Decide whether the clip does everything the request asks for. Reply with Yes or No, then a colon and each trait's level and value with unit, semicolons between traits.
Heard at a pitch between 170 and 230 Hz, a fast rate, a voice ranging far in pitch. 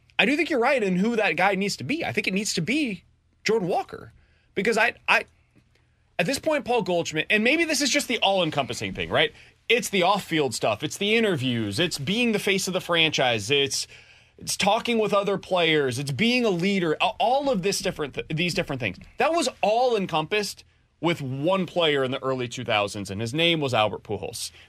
Yes: medium, 185 Hz; fast, 210 wpm; wide, 7.1 semitones